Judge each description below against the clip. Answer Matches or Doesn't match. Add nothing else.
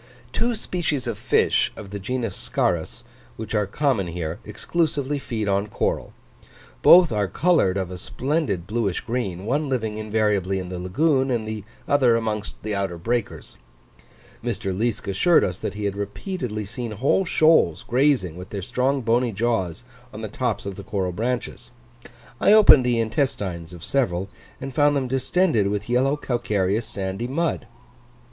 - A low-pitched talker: Matches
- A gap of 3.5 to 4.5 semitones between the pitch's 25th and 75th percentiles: Doesn't match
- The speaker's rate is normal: Matches